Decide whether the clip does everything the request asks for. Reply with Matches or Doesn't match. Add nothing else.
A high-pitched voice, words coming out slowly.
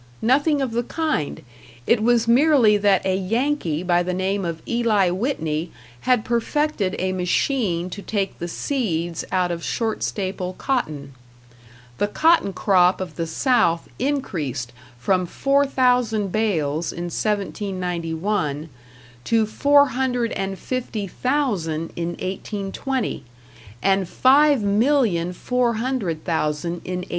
Matches